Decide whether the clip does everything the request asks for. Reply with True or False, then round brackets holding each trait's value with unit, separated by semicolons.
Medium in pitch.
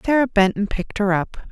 False (210 Hz)